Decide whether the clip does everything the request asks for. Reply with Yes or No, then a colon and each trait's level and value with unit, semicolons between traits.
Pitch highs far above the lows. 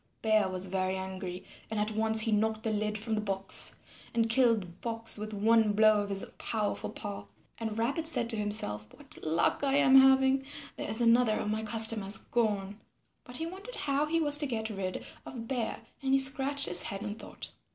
No: average, 3.3 semitones